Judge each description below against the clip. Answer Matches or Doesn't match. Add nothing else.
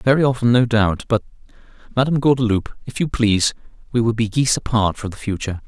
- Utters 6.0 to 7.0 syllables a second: Matches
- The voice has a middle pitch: Doesn't match